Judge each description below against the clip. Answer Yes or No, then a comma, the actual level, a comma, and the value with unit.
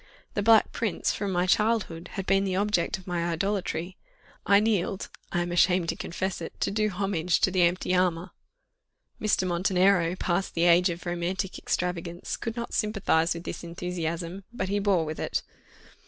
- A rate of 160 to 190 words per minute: Yes, average, 175 wpm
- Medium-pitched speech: Yes, medium, 180 Hz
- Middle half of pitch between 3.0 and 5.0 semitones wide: No, narrow, 2.5 semitones